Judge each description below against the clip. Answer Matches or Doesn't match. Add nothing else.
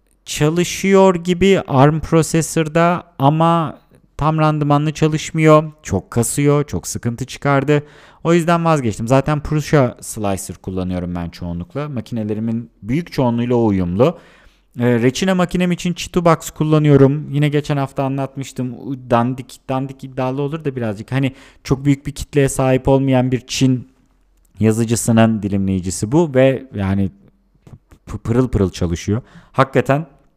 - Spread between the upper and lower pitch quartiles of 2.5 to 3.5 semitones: Doesn't match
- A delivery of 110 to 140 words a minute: Matches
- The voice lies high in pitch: Doesn't match